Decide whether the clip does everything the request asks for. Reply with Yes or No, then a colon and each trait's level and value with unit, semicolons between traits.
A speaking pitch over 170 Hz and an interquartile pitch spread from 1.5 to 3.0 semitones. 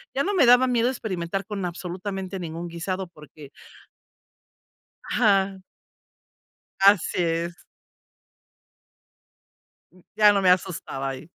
No: high, 190 Hz; average, 3.4 semitones